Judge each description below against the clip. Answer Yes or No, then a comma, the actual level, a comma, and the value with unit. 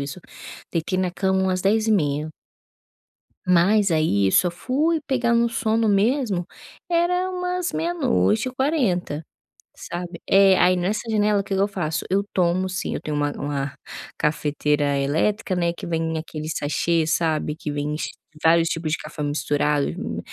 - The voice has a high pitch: No, medium, 180 Hz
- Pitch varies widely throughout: Yes, wide, 5.9 semitones